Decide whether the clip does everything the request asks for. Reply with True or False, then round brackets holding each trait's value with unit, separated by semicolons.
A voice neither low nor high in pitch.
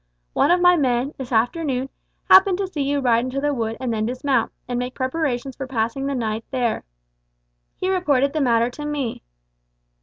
False (265 Hz)